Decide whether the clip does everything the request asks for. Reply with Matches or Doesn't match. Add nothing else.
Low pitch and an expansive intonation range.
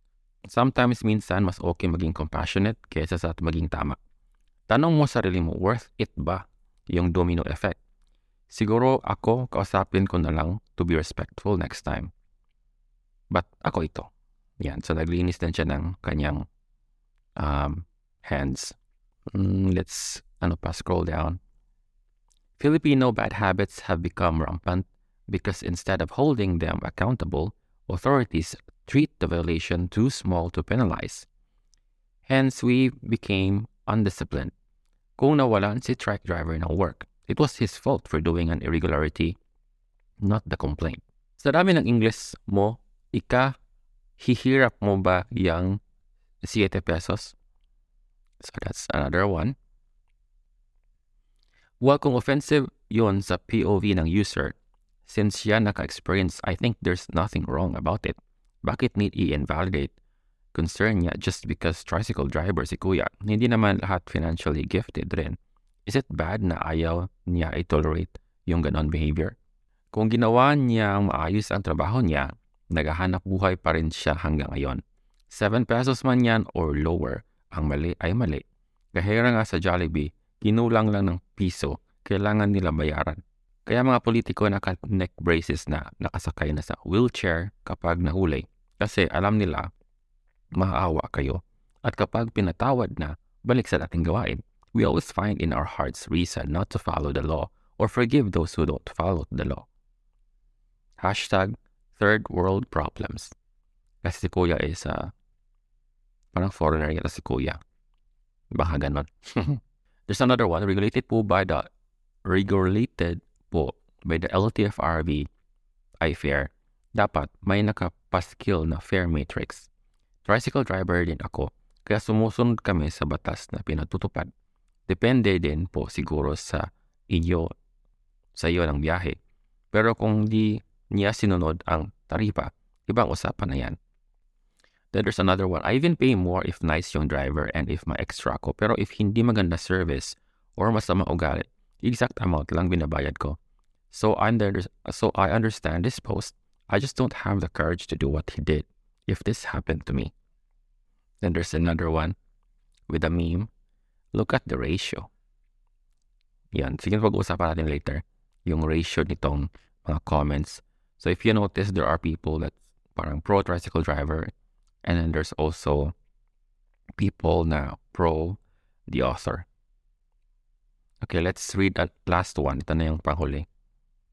Doesn't match